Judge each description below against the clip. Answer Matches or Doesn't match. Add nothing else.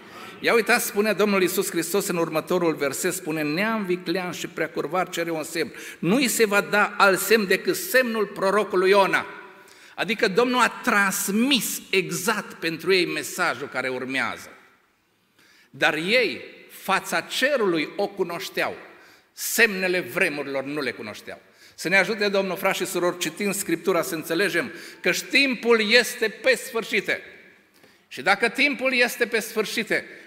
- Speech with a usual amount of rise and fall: Matches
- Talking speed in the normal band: Matches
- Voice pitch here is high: Matches